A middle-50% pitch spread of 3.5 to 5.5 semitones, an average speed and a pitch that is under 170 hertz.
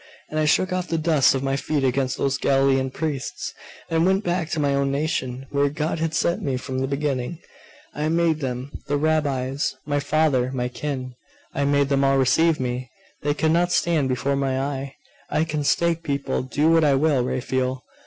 No: average, 2.9 semitones; average, 195 wpm; medium, 140 Hz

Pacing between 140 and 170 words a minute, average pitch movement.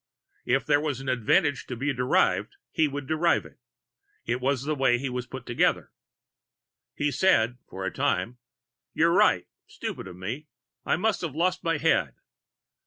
Yes: average, 165 wpm; average, 4.1 semitones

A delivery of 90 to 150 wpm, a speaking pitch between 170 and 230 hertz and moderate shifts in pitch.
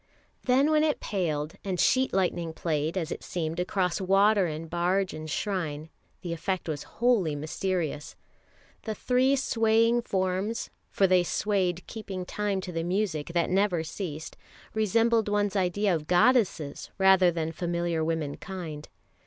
Yes: average, 145 wpm; medium, 185 Hz; average, 4.0 semitones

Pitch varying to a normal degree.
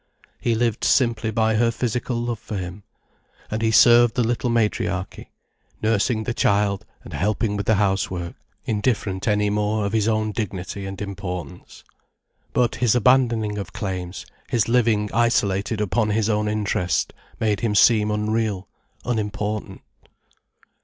No: narrow, 2.3 semitones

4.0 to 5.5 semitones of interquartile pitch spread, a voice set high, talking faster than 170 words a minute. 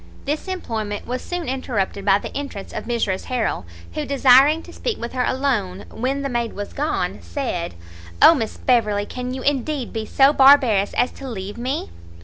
Yes: average, 4.9 semitones; very high, 250 Hz; average, 180 wpm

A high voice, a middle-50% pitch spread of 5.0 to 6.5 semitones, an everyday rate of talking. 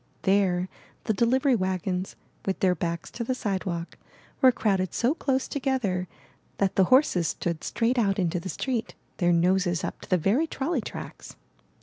Yes: high, 195 Hz; wide, 5.5 semitones; average, 160 wpm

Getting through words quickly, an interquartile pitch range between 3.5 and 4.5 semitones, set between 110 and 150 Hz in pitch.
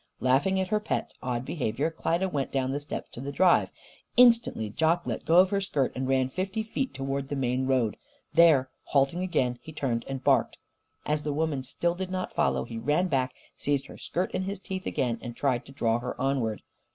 No: fast, 210 wpm; wide, 5.5 semitones; medium, 140 Hz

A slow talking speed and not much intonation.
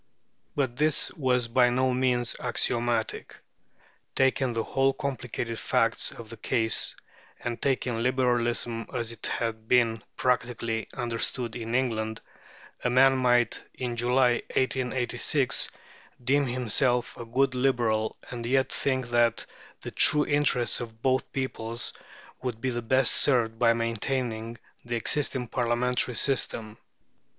Yes: slow, 125 wpm; narrow, 2.0 semitones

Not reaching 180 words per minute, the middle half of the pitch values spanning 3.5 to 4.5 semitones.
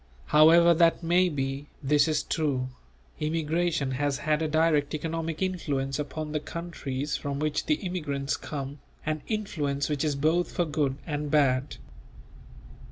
No: average, 145 wpm; average, 2.7 semitones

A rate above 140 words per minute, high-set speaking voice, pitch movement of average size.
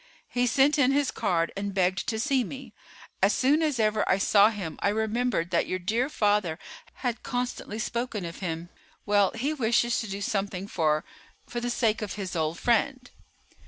Yes: average, 180 wpm; high, 215 Hz; average, 4.4 semitones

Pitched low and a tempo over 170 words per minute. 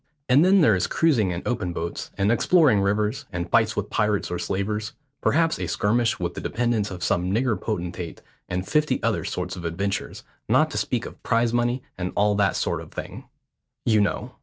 Yes: low, 105 Hz; average, 195 wpm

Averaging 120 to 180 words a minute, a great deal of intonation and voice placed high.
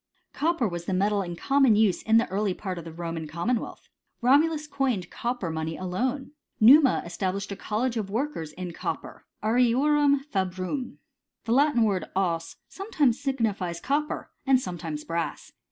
Yes: average, 155 wpm; wide, 7.0 semitones; high, 215 Hz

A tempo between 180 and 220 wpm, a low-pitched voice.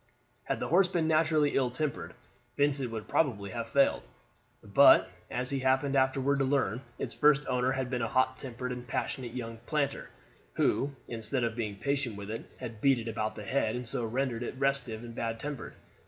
Yes: average, 195 wpm; low, 130 Hz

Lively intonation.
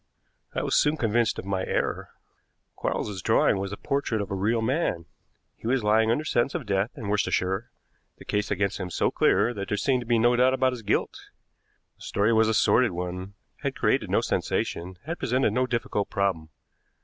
No: average, 3.8 semitones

